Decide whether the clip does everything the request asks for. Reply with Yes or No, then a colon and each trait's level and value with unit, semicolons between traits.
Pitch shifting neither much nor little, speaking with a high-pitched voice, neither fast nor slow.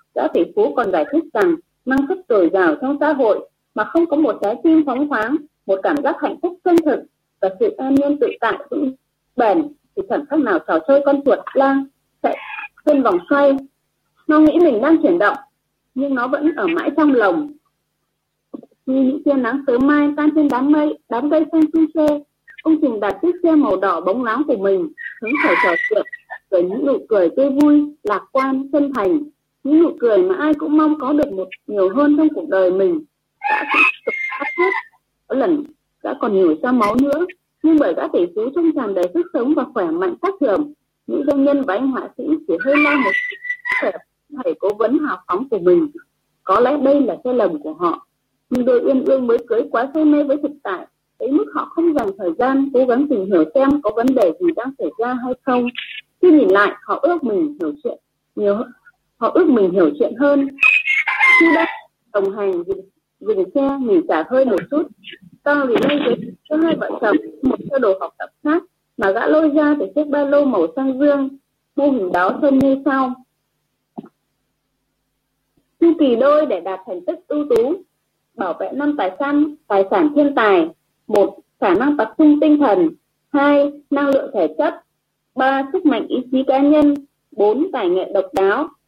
Yes: average, 3.7 semitones; very high, 290 Hz; average, 205 wpm